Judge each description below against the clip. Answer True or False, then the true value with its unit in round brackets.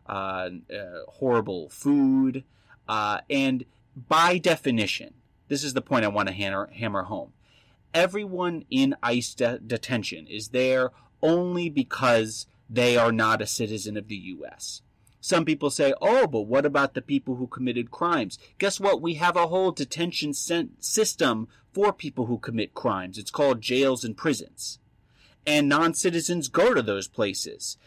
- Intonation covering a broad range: True (6.2 semitones)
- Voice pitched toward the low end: True (130 Hz)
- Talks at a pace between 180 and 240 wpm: False (155 wpm)